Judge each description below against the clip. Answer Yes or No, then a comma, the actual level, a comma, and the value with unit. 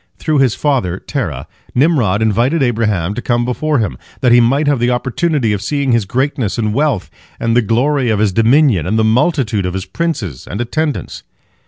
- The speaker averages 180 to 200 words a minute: Yes, average, 190 wpm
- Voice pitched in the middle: No, low, 120 Hz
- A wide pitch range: No, average, 4.9 semitones